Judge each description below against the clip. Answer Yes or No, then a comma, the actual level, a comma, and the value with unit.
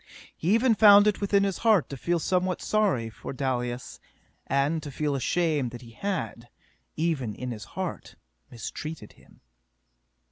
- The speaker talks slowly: No, average, 150 wpm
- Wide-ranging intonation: Yes, wide, 7.7 semitones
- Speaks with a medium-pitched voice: Yes, medium, 155 Hz